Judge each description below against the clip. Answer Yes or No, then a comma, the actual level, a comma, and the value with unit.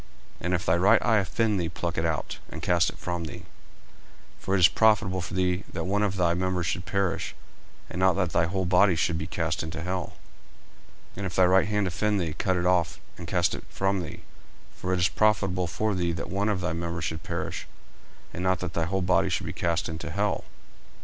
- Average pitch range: No, narrow, 2.2 semitones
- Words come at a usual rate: No, fast, 230 wpm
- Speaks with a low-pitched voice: Yes, very low, 90 Hz